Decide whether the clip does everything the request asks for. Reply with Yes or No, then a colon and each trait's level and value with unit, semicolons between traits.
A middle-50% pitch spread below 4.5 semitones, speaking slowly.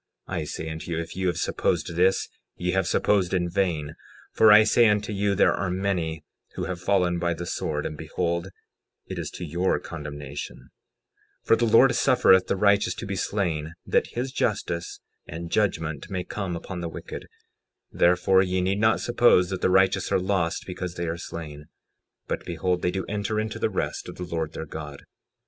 No: average, 2.9 semitones; average, 195 wpm